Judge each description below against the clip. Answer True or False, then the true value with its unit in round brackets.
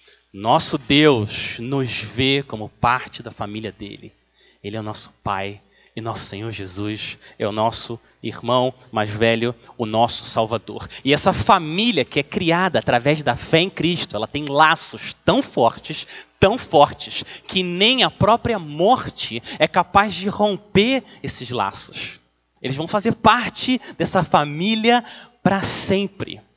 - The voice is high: False (140 Hz)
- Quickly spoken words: False (145 wpm)